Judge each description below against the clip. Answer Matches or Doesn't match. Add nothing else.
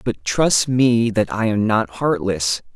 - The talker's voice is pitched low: Matches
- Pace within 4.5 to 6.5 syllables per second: Doesn't match